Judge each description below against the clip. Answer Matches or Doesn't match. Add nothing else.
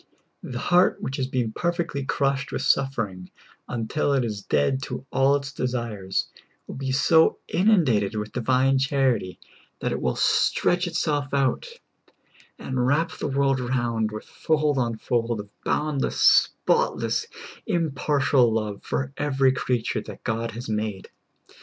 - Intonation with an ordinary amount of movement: Matches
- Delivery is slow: Doesn't match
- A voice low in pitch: Matches